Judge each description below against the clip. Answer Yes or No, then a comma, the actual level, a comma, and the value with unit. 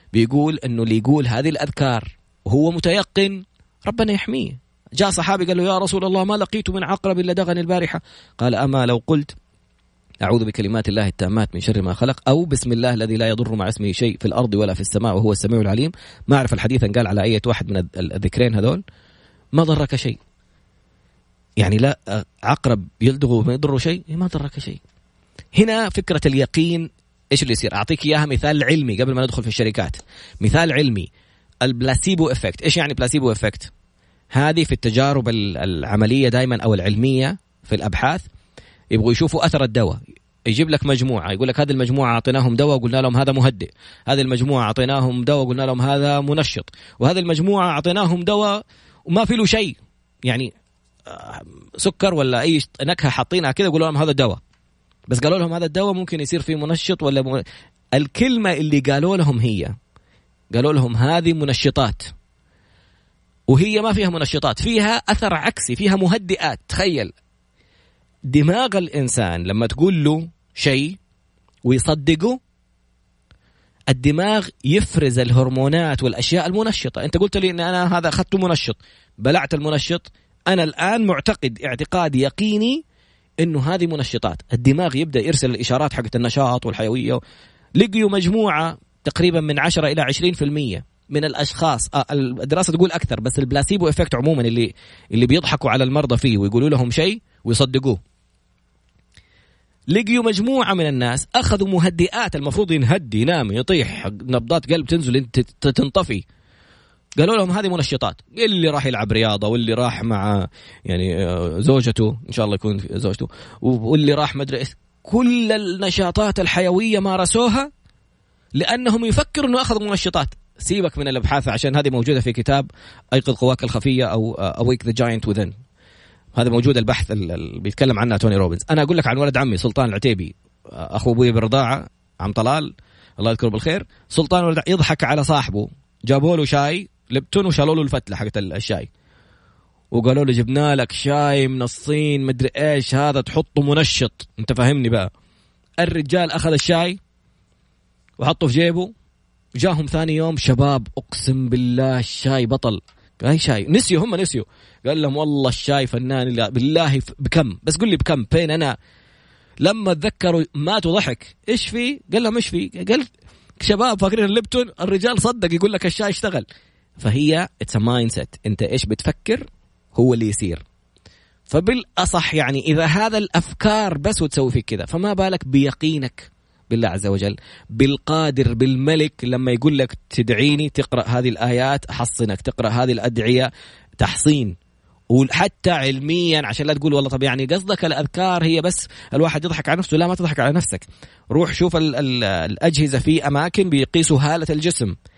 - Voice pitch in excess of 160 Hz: No, medium, 140 Hz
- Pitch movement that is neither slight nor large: No, wide, 6.1 semitones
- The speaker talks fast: Yes, fast, 145 wpm